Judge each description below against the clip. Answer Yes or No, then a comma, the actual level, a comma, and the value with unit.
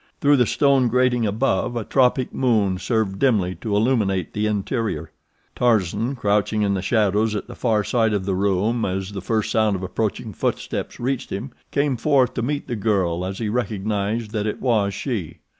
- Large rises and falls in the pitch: No, average, 3.5 semitones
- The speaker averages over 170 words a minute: Yes, average, 185 wpm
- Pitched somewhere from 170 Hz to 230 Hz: No, low, 110 Hz